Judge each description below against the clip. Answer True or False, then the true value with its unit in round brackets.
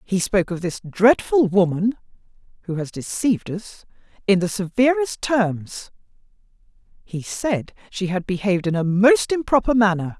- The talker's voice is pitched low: False (205 Hz)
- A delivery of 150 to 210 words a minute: False (140 wpm)